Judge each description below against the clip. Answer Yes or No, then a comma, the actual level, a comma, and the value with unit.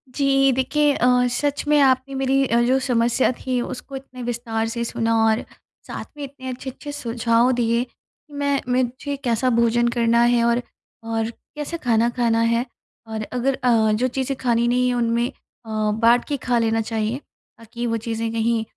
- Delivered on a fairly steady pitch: Yes, narrow, 2.3 semitones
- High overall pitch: Yes, high, 240 Hz